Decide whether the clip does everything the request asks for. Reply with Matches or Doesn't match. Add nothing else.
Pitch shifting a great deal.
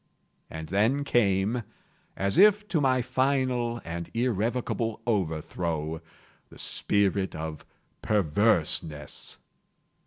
Matches